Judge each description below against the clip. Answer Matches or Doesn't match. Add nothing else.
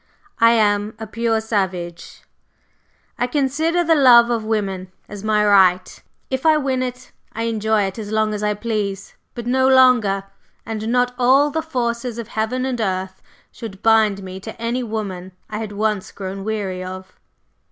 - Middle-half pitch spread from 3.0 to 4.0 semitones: Matches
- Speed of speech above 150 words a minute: Matches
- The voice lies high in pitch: Matches